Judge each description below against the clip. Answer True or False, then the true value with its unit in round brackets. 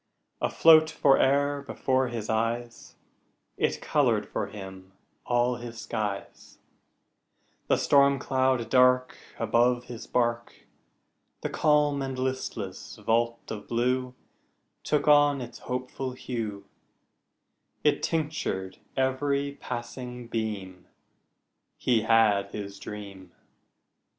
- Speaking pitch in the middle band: False (125 Hz)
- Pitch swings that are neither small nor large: True (3.3 semitones)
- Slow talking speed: True (100 wpm)